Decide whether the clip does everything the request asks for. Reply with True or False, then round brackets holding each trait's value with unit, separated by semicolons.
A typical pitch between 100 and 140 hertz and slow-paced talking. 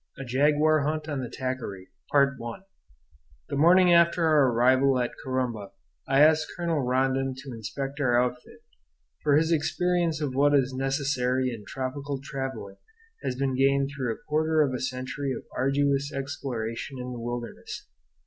False (135 Hz; 155 wpm)